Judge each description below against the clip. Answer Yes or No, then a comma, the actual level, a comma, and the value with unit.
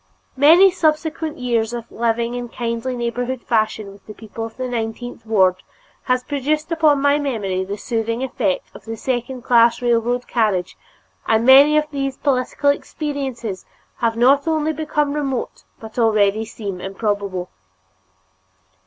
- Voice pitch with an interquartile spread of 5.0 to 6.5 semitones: No, average, 3.9 semitones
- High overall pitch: Yes, high, 240 Hz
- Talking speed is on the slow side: No, average, 145 wpm